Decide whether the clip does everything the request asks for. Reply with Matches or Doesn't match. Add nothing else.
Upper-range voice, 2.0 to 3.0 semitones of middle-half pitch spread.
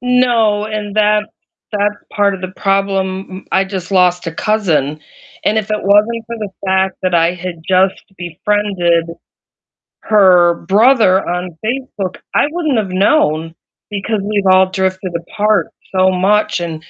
Matches